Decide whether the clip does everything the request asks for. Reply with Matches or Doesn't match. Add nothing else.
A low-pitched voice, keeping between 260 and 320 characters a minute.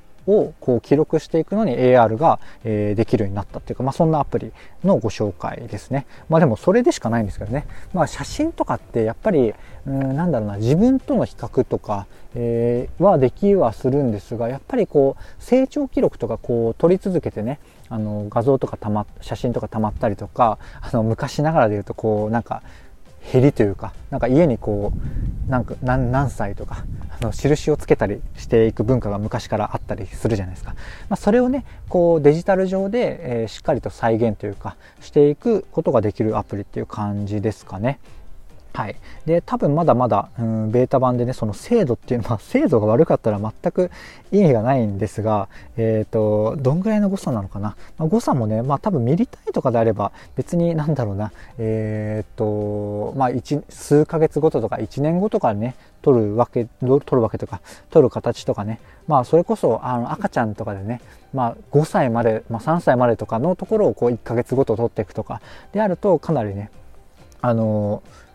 Doesn't match